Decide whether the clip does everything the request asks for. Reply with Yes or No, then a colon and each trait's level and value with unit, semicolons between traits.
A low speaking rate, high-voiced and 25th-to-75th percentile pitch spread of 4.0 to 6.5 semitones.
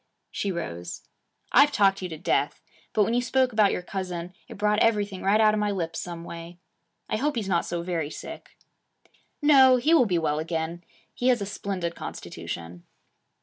No: average, 190 wpm; high, 195 Hz; average, 4.4 semitones